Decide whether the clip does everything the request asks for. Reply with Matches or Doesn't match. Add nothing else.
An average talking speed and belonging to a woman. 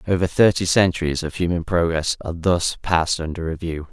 Doesn't match